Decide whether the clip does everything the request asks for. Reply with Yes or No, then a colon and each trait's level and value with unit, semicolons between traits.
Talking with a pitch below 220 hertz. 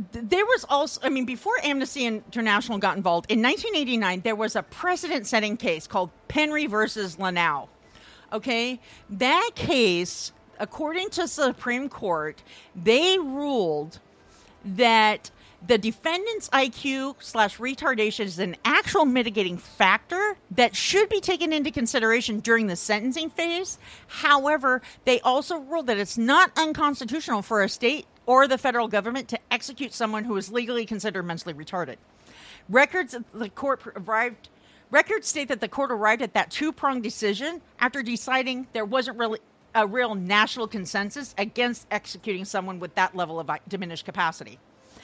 No: high, 240 Hz